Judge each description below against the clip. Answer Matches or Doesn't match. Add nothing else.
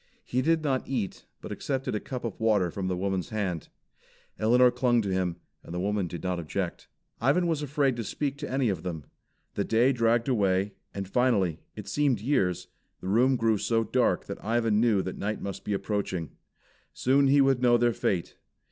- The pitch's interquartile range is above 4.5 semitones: Matches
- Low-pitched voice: Matches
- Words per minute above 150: Matches